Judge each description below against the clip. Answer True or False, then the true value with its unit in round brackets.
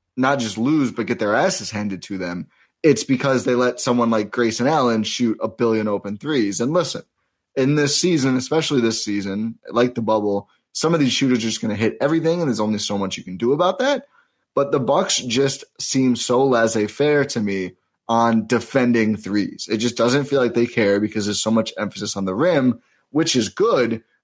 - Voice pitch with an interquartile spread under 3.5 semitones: False (3.8 semitones)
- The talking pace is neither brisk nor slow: False (210 wpm)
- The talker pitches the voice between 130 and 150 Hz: False (115 Hz)